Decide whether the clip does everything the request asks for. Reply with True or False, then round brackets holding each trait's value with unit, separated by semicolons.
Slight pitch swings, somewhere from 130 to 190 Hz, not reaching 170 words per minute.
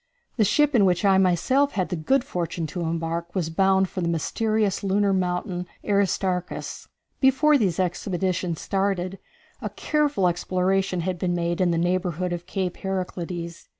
True (2.0 semitones; 185 Hz; 155 wpm)